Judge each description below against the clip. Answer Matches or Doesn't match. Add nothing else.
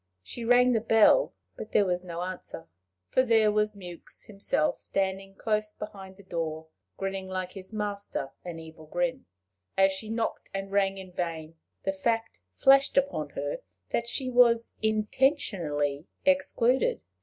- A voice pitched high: Matches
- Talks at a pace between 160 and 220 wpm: Doesn't match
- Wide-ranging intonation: Doesn't match